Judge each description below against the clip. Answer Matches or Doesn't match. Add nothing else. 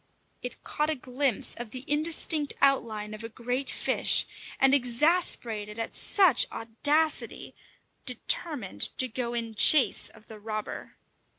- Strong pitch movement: Doesn't match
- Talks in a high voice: Matches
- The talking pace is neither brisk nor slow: Doesn't match